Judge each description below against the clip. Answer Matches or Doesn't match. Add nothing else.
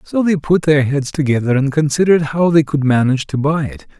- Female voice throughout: Doesn't match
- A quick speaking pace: Matches